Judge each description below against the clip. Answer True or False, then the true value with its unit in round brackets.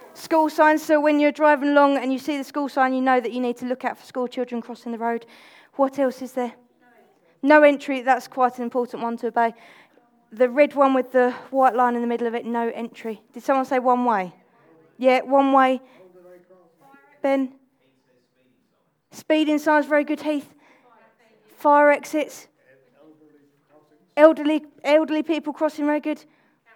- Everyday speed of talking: True (170 wpm)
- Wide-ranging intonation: False (3.8 semitones)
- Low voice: False (260 Hz)